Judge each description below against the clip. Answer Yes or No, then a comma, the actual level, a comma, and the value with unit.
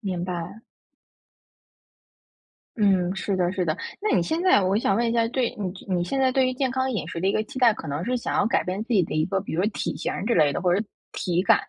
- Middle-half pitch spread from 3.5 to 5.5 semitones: Yes, average, 4.9 semitones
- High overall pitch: Yes, high, 200 Hz